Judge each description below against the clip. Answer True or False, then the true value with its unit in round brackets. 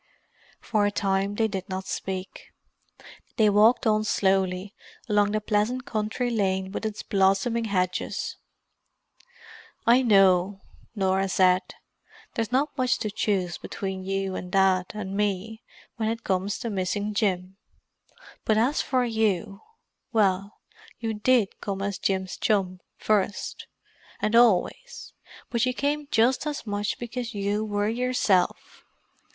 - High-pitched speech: True (205 Hz)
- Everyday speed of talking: False (130 wpm)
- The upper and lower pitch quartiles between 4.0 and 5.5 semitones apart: False (2.9 semitones)